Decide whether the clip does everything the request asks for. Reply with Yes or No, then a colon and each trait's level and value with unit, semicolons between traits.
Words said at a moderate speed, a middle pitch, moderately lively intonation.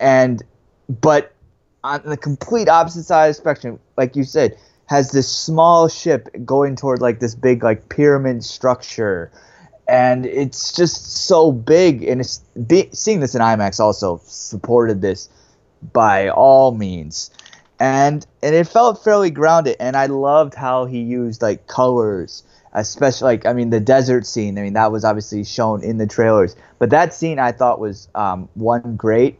No: average, 165 wpm; low, 125 Hz; average, 4.5 semitones